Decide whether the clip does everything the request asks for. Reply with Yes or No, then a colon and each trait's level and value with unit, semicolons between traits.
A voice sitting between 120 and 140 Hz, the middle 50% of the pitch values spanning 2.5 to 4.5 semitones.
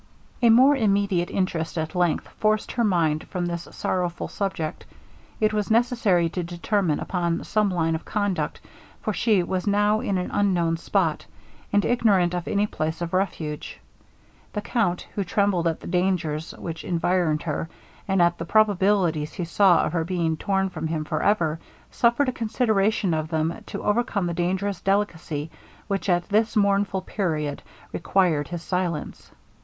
No: medium, 185 Hz; average, 3.5 semitones